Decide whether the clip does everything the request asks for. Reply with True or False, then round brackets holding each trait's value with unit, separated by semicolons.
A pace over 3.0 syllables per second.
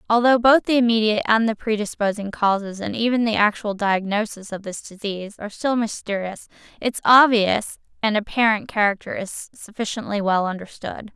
True (5.4 syllables/s)